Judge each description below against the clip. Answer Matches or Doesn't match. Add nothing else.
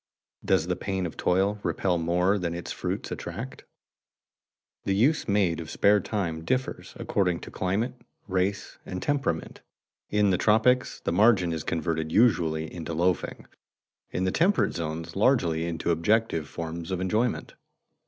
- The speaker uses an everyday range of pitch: Matches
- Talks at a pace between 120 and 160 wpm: Matches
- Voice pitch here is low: Matches